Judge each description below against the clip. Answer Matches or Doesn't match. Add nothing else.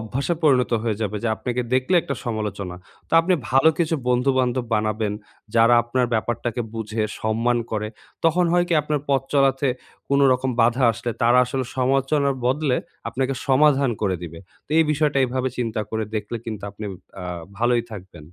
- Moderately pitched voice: Doesn't match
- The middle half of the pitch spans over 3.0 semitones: Matches